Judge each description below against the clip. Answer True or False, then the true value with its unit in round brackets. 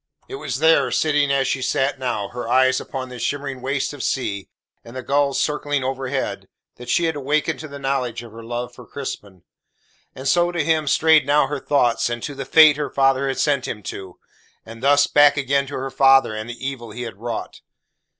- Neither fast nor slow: False (210 wpm)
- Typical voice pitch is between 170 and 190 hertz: False (135 Hz)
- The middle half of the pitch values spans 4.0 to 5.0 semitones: False (2.8 semitones)